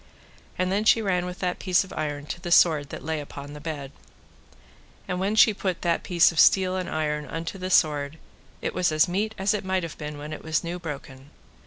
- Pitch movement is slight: No, average, 3.7 semitones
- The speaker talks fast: Yes, fast, 220 wpm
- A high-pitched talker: No, medium, 170 Hz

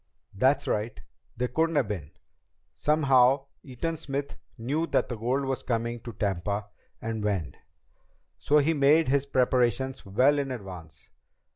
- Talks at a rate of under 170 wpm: Yes, average, 140 wpm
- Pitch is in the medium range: No, low, 125 Hz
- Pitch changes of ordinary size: Yes, average, 4.8 semitones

